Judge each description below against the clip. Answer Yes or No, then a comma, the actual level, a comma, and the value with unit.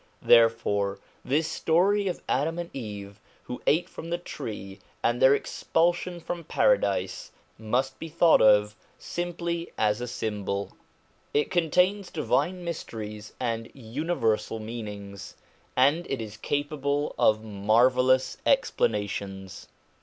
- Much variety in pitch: Yes, wide, 7.7 semitones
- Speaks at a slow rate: Yes, slow, 115 wpm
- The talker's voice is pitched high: No, low, 130 Hz